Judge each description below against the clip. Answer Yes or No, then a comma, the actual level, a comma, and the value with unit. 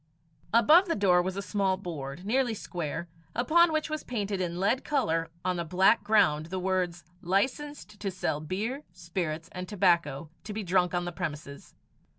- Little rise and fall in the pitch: No, average, 4.2 semitones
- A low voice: No, medium, 185 Hz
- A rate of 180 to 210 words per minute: No, average, 170 wpm